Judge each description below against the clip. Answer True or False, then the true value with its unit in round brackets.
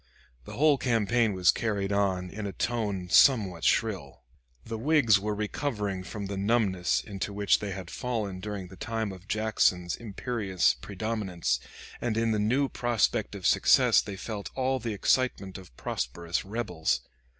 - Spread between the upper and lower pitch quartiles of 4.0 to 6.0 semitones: False (3.3 semitones)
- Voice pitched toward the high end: False (105 Hz)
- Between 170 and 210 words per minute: False (155 wpm)